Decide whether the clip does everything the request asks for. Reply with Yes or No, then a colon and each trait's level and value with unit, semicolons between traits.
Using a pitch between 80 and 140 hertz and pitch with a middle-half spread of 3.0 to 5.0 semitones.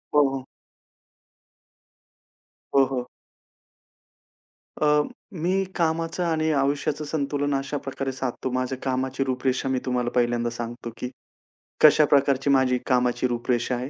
No: low, 135 Hz; narrow, 2.6 semitones